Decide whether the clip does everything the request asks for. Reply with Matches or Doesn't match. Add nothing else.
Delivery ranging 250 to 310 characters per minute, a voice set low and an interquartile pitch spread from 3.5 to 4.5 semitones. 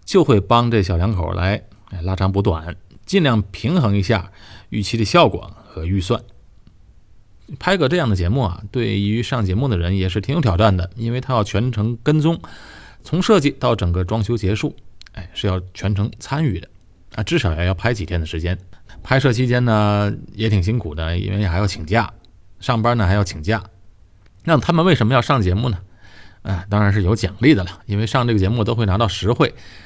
Matches